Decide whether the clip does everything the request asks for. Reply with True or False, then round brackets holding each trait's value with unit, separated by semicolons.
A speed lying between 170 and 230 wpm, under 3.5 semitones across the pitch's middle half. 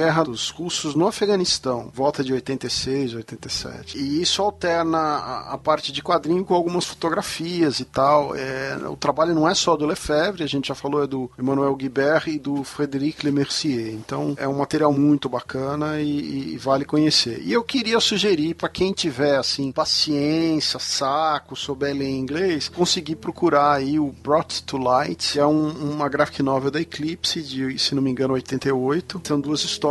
True (180 wpm; 3.0 semitones)